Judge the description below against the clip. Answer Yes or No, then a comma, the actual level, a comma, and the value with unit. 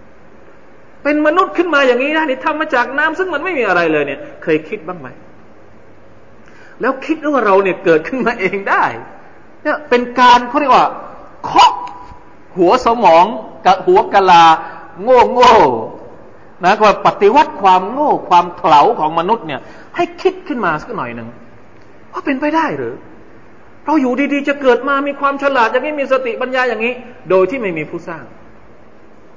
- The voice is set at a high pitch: Yes, high, 245 Hz